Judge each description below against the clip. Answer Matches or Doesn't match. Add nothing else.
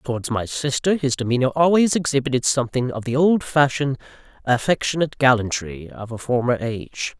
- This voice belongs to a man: Matches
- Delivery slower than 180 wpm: Matches